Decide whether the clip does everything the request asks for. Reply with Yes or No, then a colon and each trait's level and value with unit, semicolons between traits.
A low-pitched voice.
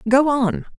No: very high, 260 Hz